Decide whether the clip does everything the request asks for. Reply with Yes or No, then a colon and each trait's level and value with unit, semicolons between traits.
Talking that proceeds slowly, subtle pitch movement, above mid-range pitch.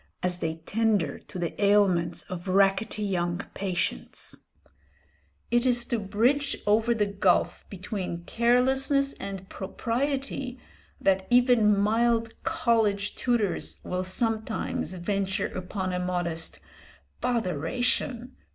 No: slow, 105 wpm; average, 4.4 semitones; high, 205 Hz